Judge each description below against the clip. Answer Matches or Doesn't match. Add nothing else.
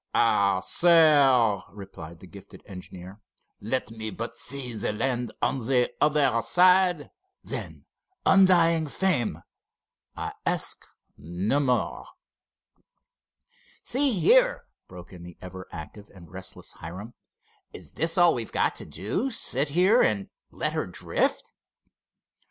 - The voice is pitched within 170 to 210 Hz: Doesn't match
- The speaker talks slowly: Matches